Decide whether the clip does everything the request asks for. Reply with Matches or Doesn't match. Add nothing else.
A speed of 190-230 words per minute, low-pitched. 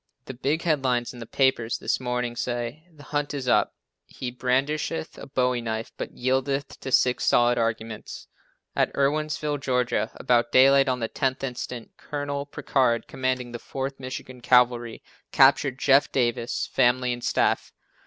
Doesn't match